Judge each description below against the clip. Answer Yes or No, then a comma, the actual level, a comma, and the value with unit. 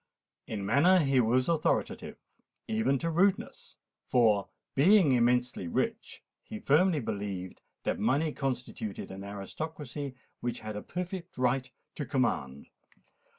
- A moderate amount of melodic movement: No, wide, 6.8 semitones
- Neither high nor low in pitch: No, low, 130 Hz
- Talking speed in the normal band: No, slow, 120 wpm